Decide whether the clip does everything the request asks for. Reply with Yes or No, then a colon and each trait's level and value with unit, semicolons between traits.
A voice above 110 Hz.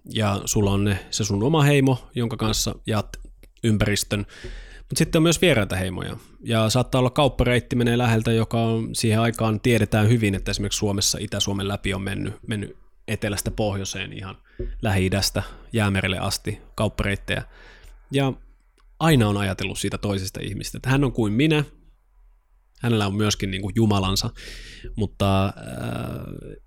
No: low, 105 Hz